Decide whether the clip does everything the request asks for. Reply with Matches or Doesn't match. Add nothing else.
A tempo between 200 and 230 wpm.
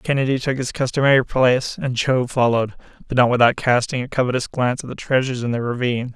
Matches